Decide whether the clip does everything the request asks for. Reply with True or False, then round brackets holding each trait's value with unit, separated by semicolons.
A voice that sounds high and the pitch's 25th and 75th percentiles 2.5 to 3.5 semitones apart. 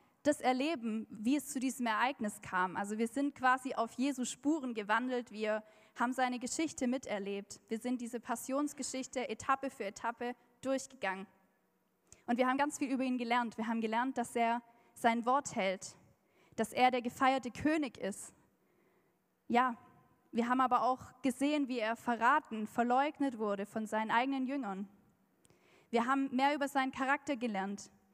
True (245 Hz; 3.0 semitones)